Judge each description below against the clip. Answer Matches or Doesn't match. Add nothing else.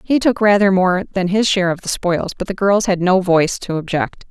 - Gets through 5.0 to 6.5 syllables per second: Matches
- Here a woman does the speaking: Matches